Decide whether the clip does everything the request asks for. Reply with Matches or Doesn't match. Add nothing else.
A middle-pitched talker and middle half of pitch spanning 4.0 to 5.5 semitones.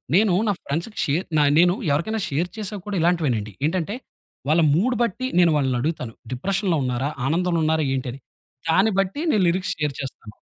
Matches